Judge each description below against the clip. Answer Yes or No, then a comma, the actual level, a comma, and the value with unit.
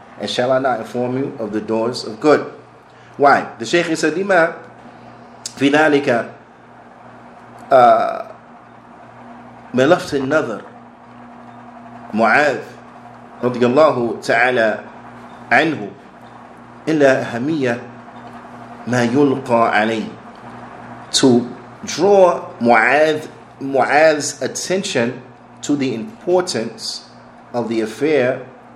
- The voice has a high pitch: No, low, 135 Hz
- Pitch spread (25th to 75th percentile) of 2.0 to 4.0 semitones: No, average, 5.0 semitones